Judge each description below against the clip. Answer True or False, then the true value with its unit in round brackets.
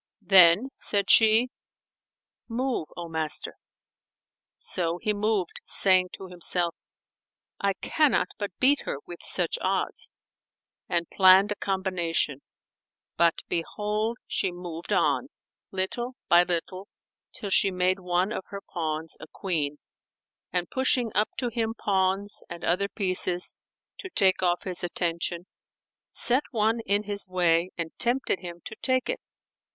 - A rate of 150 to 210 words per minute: False (135 wpm)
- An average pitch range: True (3.3 semitones)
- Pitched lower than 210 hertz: True (190 Hz)